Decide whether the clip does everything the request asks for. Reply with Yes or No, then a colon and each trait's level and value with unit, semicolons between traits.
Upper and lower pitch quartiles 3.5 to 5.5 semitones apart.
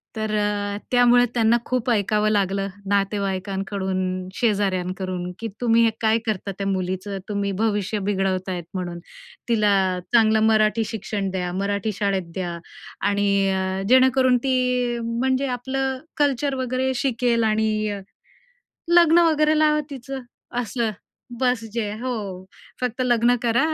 Yes: average, 4.0 semitones